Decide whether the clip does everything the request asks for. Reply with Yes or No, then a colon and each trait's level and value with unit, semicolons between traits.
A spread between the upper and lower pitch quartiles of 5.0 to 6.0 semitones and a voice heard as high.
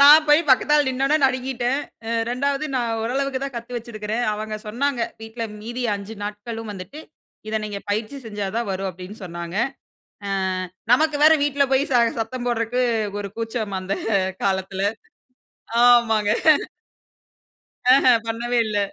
No: average, 3.9 semitones; high, 235 Hz